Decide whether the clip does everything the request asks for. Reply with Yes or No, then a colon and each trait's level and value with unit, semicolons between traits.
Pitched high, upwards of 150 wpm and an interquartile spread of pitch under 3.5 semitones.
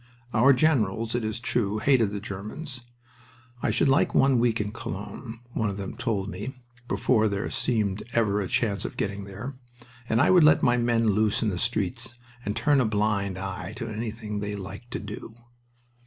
No: low, 110 Hz; average, 185 wpm; average, 3.0 semitones